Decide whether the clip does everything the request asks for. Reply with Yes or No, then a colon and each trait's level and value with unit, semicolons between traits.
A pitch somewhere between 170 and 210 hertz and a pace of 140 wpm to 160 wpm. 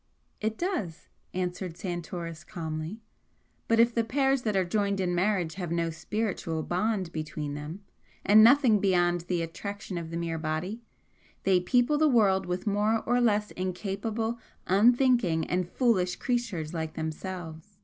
Yes: medium, 185 Hz; average, 150 wpm